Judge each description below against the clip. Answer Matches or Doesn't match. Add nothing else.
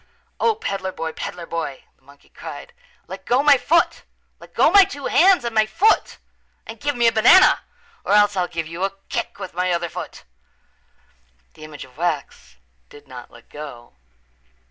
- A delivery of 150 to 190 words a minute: Matches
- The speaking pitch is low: Doesn't match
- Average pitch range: Doesn't match